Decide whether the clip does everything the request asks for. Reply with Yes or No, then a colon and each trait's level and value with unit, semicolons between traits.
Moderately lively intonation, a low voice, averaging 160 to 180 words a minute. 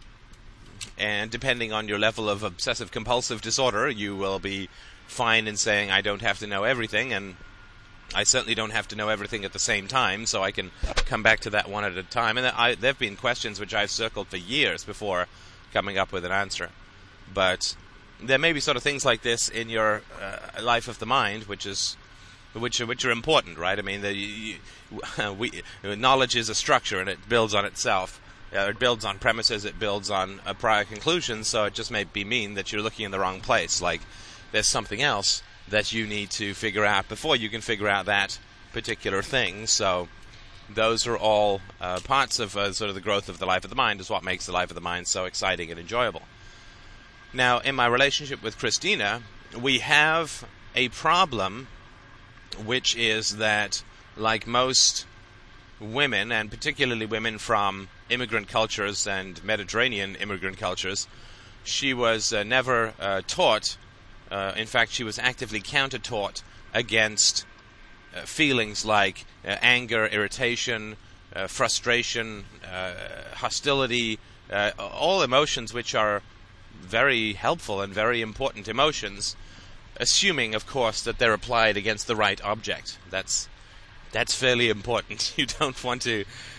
Yes: average, 3.0 semitones; low, 105 Hz; average, 170 wpm